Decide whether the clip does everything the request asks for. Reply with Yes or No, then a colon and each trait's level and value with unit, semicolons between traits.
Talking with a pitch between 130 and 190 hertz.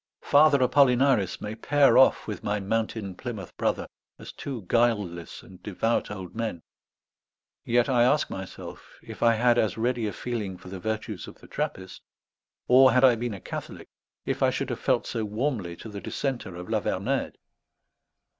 No: low, 110 Hz